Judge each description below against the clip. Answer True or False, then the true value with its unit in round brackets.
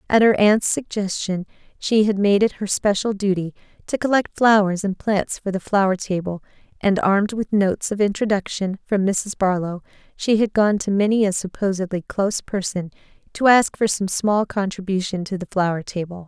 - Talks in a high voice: True (200 Hz)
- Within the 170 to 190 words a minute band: True (175 wpm)